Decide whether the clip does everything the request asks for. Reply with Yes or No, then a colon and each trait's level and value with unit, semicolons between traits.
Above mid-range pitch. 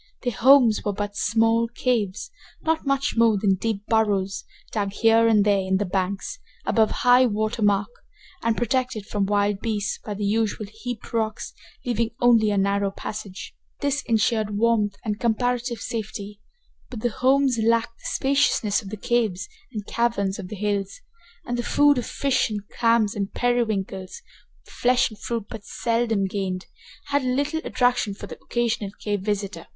Yes: high, 220 Hz